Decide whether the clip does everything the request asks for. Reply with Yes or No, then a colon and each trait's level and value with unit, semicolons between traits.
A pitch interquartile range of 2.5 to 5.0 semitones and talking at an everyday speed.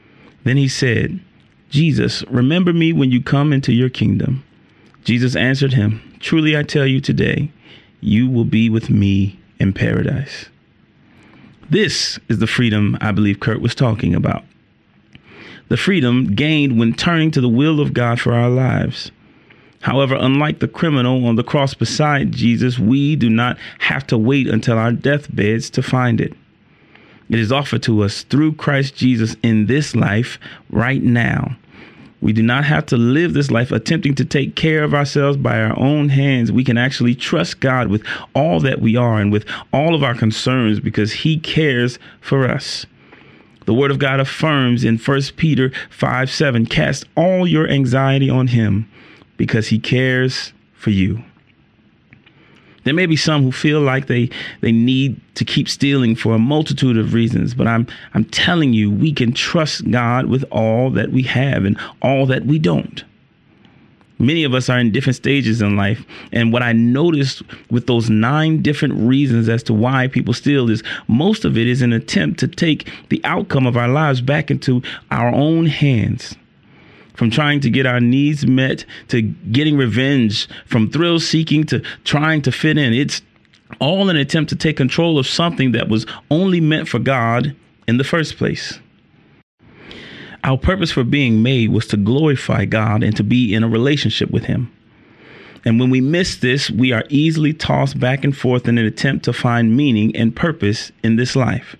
Yes: average, 3.9 semitones; average, 175 wpm